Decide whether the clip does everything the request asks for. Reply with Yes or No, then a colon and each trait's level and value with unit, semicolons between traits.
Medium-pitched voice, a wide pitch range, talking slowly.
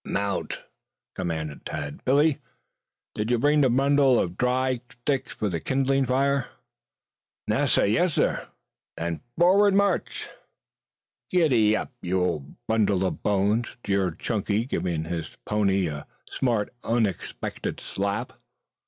No: low, 110 Hz; wide, 6.3 semitones; slow, 115 wpm